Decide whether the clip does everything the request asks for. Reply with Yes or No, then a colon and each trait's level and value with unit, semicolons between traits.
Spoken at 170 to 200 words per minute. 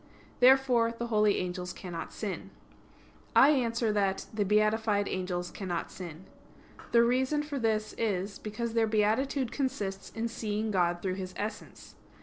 No: average, 140 wpm